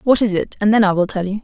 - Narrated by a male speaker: No, female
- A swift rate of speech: Yes, fast, 375 wpm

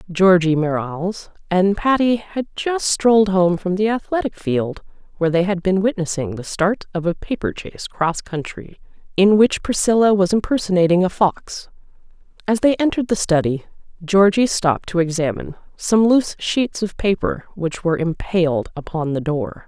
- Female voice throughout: Yes, female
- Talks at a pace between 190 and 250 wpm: No, average, 160 wpm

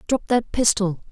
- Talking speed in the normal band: Yes, average, 160 wpm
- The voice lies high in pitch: Yes, high, 220 Hz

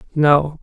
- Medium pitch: Yes, medium, 150 Hz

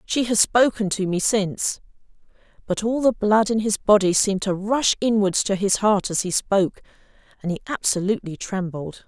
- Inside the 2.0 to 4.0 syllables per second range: No, 5.1 syllables/s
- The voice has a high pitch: Yes, high, 205 Hz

